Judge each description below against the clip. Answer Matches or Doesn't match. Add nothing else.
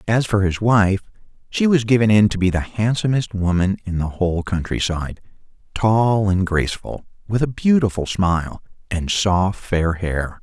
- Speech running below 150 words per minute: Doesn't match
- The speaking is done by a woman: Doesn't match